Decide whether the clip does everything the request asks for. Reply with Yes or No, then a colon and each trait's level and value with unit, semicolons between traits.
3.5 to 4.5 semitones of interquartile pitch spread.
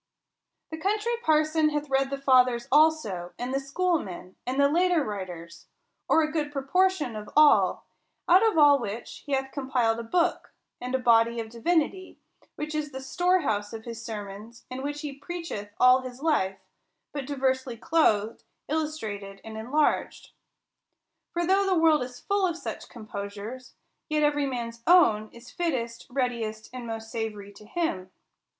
No: wide, 5.6 semitones